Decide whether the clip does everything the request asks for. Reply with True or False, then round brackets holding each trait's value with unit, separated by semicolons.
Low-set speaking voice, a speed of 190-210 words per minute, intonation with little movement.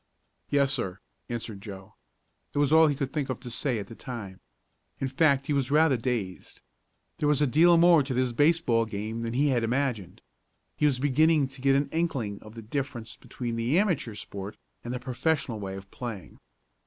False (130 Hz; 195 wpm; 4.3 semitones)